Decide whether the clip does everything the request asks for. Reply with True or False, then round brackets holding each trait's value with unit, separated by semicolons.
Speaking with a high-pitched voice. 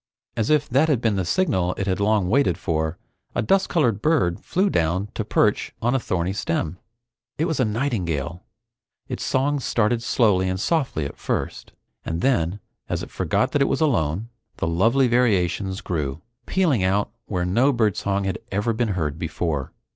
False (100 Hz)